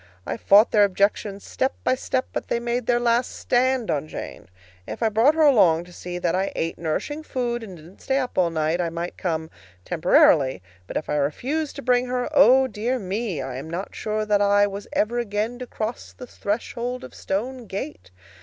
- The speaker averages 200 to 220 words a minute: Yes, fast, 205 wpm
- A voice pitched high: Yes, high, 210 Hz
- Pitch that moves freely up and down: Yes, wide, 6.0 semitones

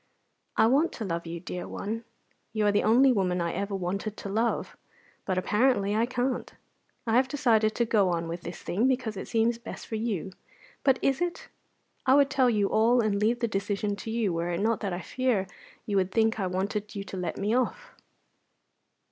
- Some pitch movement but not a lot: Yes, average, 3.5 semitones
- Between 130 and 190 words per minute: No, fast, 205 wpm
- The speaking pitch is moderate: No, high, 215 Hz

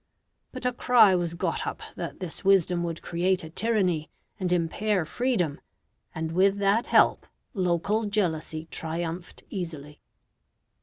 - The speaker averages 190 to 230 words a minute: No, slow, 135 wpm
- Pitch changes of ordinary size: Yes, average, 3.7 semitones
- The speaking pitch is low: No, medium, 180 Hz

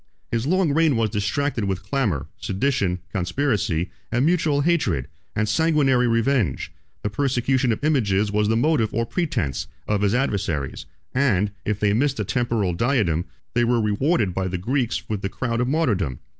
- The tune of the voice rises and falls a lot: Yes, wide, 5.8 semitones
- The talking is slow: No, average, 165 wpm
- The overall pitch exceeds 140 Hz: No, low, 115 Hz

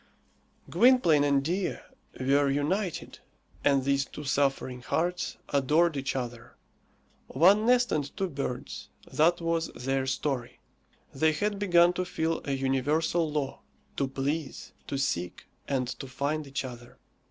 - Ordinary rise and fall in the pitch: Yes, average, 3.8 semitones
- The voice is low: No, medium, 145 Hz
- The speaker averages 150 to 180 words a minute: No, slow, 135 wpm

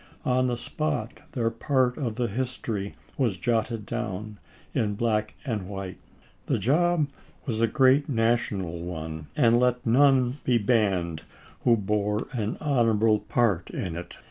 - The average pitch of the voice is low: Yes, low, 115 Hz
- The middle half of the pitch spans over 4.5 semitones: No, average, 3.6 semitones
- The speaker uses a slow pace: No, average, 145 wpm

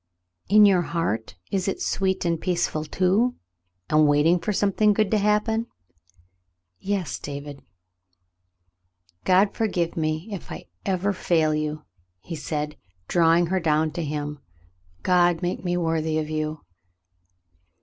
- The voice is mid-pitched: Yes, medium, 170 Hz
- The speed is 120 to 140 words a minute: Yes, slow, 135 wpm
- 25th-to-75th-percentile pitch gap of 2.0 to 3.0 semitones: No, average, 3.8 semitones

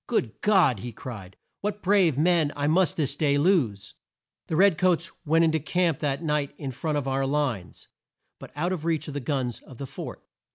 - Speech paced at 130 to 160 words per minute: No, fast, 205 wpm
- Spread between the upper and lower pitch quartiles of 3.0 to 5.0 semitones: Yes, average, 4.1 semitones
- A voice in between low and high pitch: Yes, medium, 150 Hz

